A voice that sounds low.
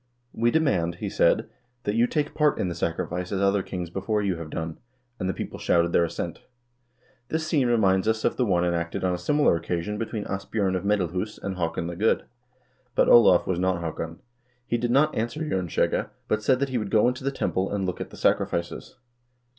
Yes: very low, 95 Hz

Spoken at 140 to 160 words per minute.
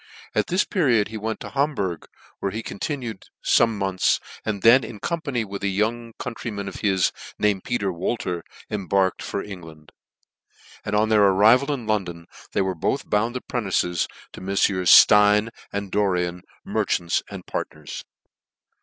Yes: average, 155 wpm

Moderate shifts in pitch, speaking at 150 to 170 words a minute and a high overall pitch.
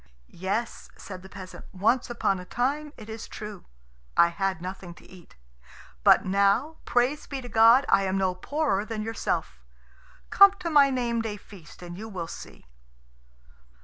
Yes: average, 4.7 semitones; average, 165 wpm; high, 215 Hz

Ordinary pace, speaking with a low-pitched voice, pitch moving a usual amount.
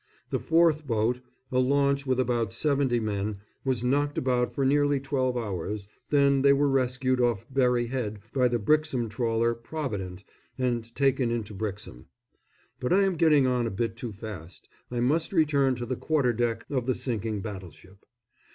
Yes: average, 170 wpm; low, 125 Hz; average, 3.6 semitones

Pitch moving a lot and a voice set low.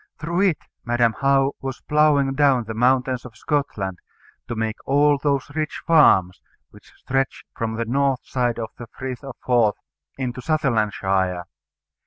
No: average, 3.6 semitones; low, 130 Hz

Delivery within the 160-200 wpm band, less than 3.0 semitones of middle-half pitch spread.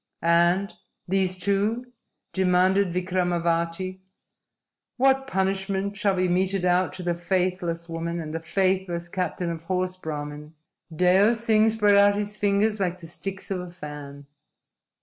No: slow, 135 wpm; narrow, 2.6 semitones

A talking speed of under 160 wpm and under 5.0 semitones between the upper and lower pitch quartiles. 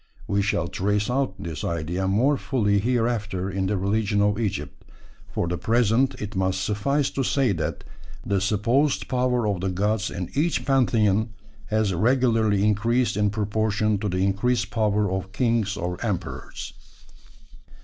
Yes: average, 150 wpm; average, 3.3 semitones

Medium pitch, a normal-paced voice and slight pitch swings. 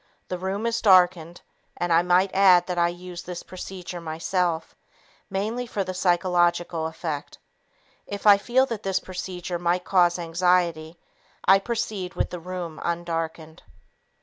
Yes: medium, 180 Hz; average, 145 wpm; narrow, 1.7 semitones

